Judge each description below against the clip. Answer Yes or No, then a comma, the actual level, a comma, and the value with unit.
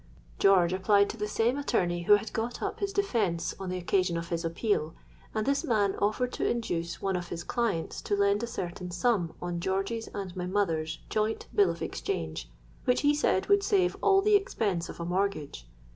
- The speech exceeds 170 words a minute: Yes, average, 200 wpm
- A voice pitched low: No, high, 195 Hz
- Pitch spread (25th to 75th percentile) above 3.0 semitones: Yes, average, 4.8 semitones